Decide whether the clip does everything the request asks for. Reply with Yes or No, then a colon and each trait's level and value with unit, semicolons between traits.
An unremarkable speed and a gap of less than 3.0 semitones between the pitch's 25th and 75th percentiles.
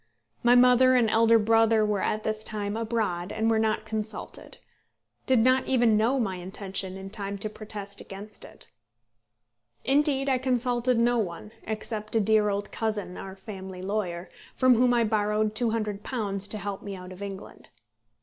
Yes: average, 165 wpm; narrow, 2.5 semitones